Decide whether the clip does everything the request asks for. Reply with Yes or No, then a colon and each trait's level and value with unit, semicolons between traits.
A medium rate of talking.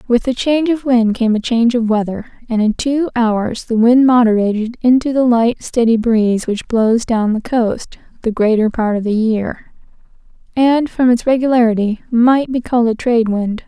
Yes: average, 190 wpm